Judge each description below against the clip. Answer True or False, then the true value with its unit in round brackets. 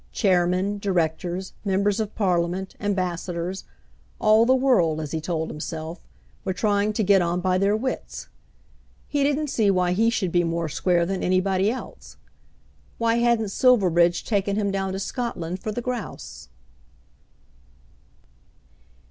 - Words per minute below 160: True (140 wpm)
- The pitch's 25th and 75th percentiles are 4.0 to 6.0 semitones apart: False (3.6 semitones)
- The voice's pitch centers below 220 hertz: True (190 Hz)